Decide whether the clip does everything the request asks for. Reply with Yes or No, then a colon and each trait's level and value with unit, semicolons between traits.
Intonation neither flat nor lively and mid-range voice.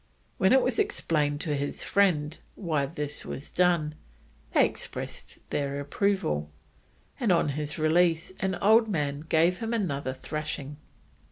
Yes: average, 4.5 semitones; medium, 155 Hz